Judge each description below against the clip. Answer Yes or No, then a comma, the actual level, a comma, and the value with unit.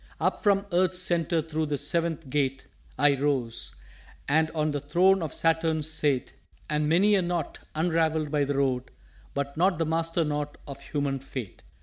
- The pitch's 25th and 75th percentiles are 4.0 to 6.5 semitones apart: No, average, 2.8 semitones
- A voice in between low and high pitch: Yes, medium, 155 Hz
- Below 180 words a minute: Yes, average, 170 wpm